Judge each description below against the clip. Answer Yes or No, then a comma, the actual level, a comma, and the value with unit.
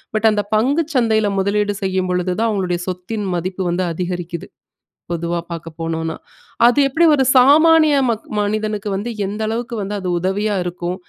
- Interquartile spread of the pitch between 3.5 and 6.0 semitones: Yes, average, 3.8 semitones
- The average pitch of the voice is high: Yes, high, 205 Hz